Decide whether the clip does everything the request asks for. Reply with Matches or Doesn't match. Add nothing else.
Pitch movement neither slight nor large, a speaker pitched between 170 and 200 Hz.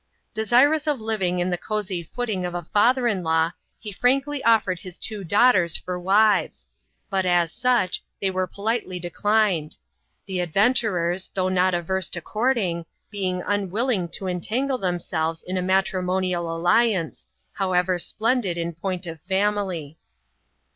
Matches